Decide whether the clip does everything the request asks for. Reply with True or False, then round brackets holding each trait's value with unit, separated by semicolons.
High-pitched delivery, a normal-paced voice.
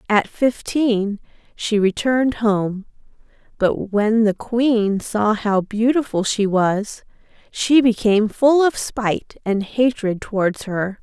False (220 Hz; 125 wpm)